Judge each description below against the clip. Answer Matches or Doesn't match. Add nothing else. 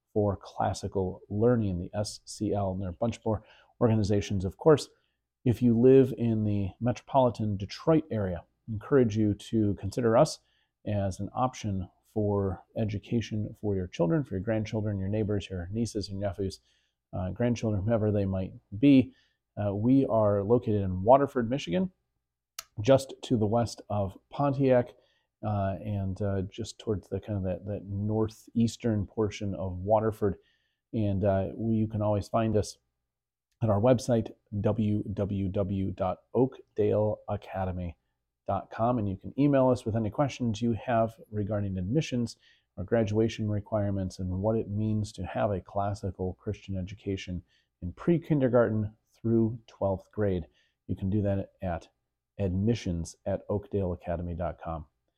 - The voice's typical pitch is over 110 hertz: Doesn't match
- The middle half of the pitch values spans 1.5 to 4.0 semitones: Matches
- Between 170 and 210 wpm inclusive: Doesn't match